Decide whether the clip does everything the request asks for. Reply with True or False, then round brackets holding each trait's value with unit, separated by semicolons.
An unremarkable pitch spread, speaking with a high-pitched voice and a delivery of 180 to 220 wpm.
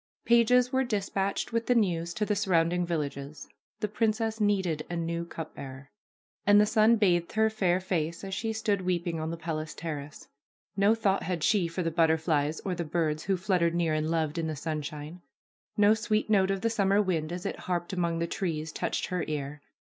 False (4.2 semitones; 175 Hz; 200 wpm)